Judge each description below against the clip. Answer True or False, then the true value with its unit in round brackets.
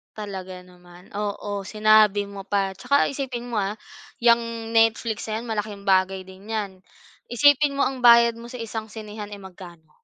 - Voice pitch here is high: True (210 Hz)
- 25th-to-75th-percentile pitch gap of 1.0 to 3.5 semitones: True (3.2 semitones)